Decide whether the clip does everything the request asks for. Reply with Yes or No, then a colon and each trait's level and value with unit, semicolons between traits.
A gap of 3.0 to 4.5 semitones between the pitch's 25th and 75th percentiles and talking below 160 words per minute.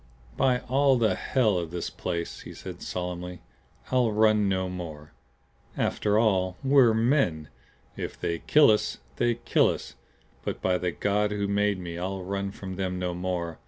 No: average, 3.7 semitones; average, 165 wpm